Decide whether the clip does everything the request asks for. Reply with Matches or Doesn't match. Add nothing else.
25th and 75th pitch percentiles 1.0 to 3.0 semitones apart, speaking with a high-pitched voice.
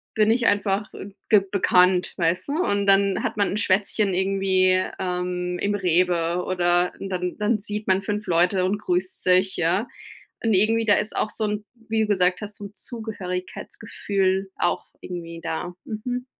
Matches